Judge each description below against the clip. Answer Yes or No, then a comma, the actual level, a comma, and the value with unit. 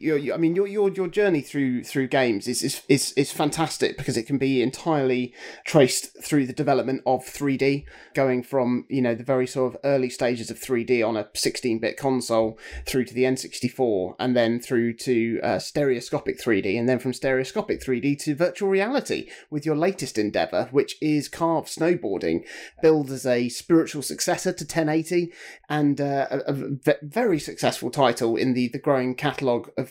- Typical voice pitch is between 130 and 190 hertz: Yes, low, 135 Hz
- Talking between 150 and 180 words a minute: Yes, average, 175 wpm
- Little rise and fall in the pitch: No, average, 3.5 semitones